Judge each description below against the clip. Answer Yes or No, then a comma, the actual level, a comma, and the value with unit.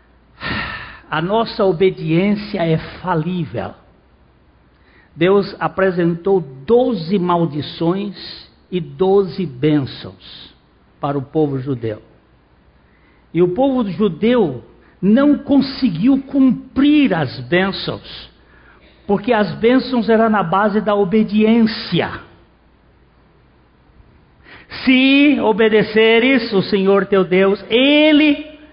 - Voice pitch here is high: Yes, high, 195 Hz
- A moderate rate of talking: No, slow, 85 wpm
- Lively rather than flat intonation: Yes, wide, 6.5 semitones